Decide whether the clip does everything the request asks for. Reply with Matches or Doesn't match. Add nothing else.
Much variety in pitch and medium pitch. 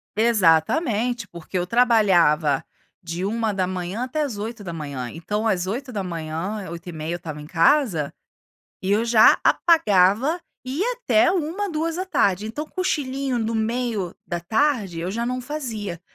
Doesn't match